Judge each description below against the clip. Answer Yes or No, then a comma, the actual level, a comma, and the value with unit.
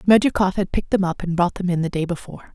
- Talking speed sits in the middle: No, fast, 285 wpm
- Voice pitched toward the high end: No, medium, 180 Hz